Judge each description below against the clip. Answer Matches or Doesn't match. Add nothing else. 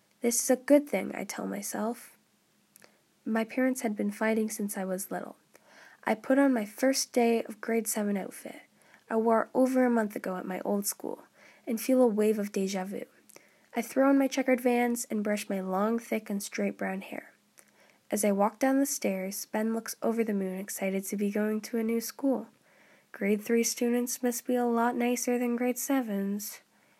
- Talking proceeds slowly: Doesn't match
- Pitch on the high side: Matches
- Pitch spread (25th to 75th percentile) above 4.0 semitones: Doesn't match